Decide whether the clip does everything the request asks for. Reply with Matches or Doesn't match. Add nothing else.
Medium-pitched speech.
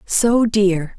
Doesn't match